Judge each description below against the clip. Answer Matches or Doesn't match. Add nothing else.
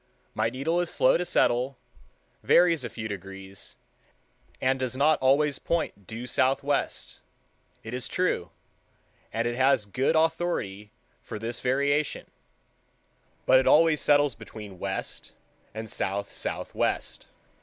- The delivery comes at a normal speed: Doesn't match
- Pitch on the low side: Matches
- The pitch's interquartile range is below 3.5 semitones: Doesn't match